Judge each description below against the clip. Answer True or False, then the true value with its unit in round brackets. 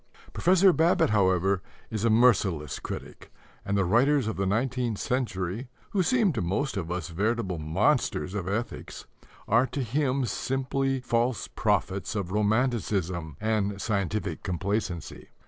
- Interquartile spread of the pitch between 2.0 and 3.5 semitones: False (5.2 semitones)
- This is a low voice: True (110 Hz)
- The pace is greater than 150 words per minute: False (135 wpm)